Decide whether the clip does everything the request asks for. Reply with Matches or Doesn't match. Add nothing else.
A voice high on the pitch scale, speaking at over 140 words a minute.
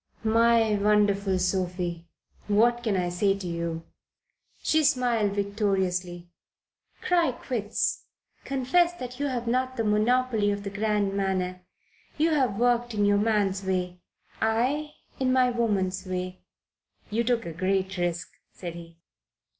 Doesn't match